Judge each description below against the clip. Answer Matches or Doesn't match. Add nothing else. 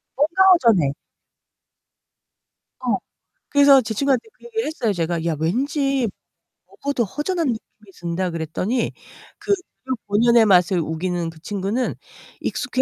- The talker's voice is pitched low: Doesn't match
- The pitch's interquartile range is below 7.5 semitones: Doesn't match